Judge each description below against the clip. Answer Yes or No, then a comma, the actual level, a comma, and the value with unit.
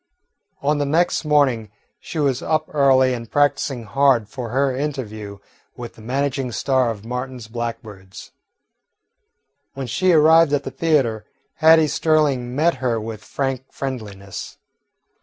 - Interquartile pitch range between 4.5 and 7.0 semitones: No, average, 3.9 semitones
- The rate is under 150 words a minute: Yes, slow, 135 wpm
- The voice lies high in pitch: No, low, 130 Hz